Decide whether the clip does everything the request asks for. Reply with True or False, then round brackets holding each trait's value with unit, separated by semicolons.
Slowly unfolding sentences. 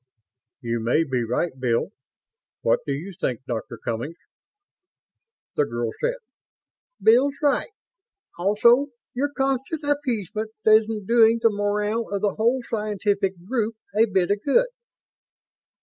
True (125 wpm)